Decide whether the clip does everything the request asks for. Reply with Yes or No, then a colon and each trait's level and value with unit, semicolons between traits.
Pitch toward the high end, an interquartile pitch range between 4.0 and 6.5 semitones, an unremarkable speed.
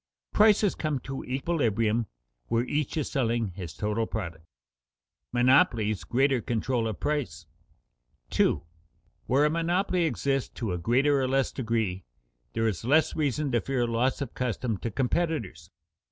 No: low, 120 Hz; average, 4.6 semitones; average, 145 wpm